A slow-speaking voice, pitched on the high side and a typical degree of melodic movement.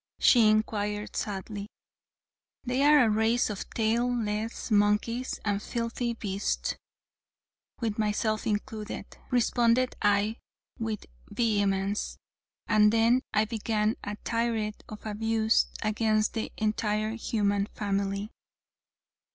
No: slow, 105 wpm; high, 215 Hz; narrow, 1.7 semitones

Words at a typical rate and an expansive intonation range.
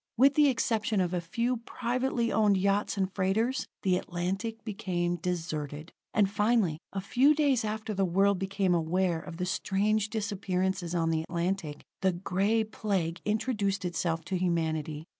No: average, 155 wpm; average, 3.8 semitones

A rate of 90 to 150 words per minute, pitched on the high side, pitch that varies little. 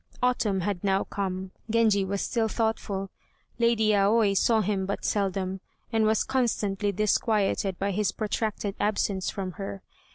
Yes: average, 140 wpm; high, 200 Hz; narrow, 2.1 semitones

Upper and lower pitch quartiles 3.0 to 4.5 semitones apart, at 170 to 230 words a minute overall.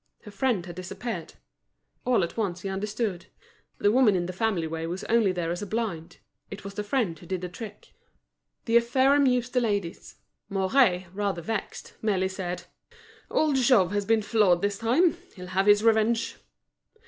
Yes: average, 4.1 semitones; average, 175 wpm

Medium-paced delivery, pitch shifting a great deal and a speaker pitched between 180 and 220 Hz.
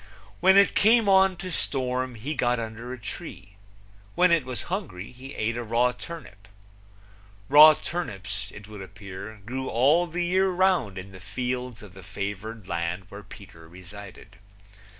No: average, 160 wpm; wide, 8.2 semitones; low, 120 Hz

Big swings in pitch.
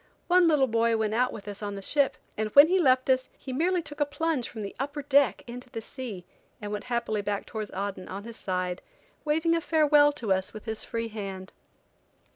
Yes: wide, 5.9 semitones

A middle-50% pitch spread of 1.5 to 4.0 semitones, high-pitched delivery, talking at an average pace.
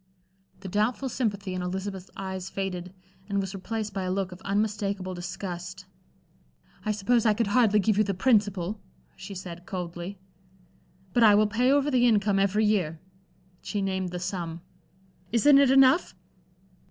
Yes: narrow, 2.6 semitones; high, 200 Hz; average, 155 wpm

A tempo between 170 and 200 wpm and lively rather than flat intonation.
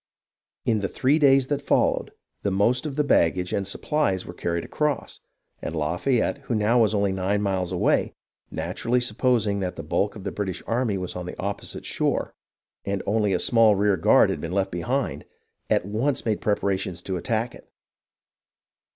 No: average, 175 wpm; average, 4.4 semitones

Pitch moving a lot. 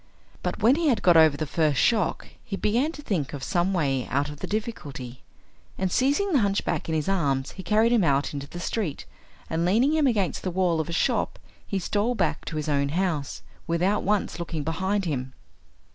Yes: wide, 6.0 semitones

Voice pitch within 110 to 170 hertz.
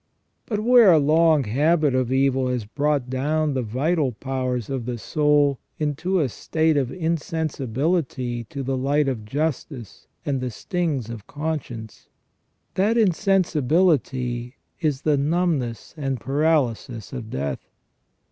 Yes: medium, 140 Hz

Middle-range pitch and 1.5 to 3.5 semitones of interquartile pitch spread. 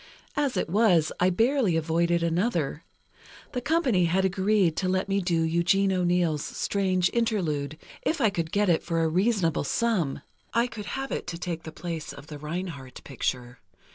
No: medium, 180 Hz; average, 3.9 semitones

